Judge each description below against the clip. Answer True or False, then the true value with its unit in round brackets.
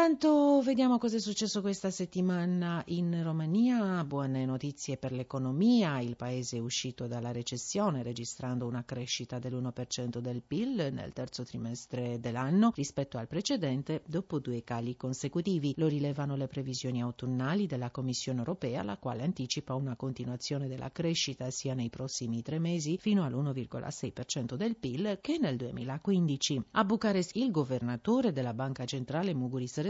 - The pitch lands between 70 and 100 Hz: False (135 Hz)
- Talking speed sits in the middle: True (140 wpm)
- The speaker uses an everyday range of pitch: False (6.0 semitones)